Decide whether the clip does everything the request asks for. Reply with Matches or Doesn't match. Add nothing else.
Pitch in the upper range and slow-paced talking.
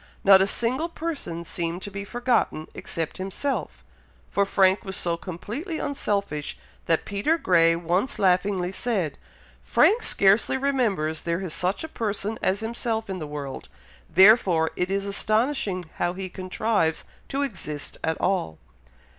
Doesn't match